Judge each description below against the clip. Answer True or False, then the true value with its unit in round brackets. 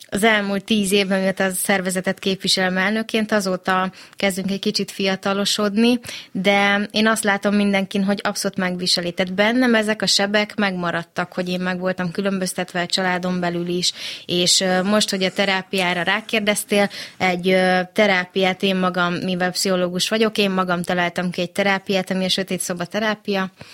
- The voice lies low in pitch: False (190 Hz)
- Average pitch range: False (1.9 semitones)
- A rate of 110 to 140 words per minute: False (150 wpm)